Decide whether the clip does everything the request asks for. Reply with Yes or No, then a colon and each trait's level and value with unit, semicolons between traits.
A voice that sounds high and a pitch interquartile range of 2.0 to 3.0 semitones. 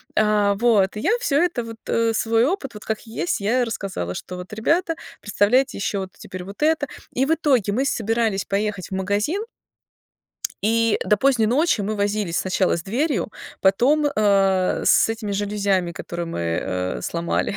No: high, 210 Hz; average, 3.7 semitones